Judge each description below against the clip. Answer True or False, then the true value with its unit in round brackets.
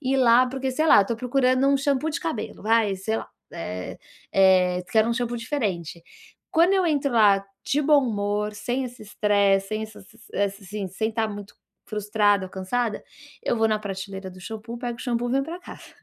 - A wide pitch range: False (4.2 semitones)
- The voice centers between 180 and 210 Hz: False (220 Hz)